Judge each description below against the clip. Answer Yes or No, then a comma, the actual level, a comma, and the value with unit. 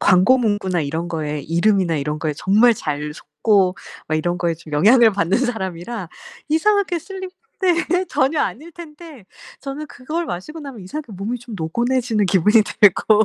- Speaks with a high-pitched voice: Yes, high, 210 Hz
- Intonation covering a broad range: Yes, wide, 8.1 semitones